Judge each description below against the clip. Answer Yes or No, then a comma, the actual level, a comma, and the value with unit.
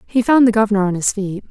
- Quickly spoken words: Yes, fast, 280 wpm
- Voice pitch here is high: Yes, high, 210 Hz